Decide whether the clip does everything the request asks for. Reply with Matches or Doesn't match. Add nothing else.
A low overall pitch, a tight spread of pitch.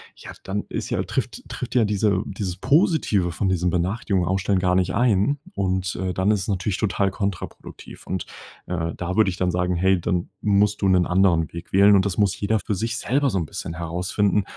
Matches